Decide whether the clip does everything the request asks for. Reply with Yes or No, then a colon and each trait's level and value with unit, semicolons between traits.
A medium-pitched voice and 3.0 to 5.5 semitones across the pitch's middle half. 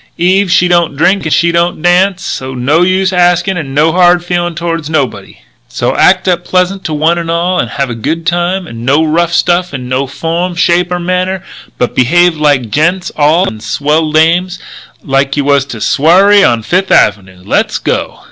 Yes: medium, 170 Hz; average, 3.9 semitones